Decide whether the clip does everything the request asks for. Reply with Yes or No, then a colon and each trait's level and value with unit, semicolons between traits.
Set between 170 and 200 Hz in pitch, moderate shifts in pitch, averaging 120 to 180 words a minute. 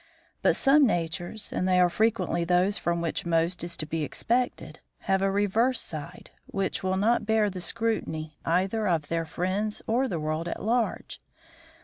Yes: medium, 185 Hz; average, 4.5 semitones; average, 170 wpm